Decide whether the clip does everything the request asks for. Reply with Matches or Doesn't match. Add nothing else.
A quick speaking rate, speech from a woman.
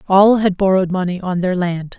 Matches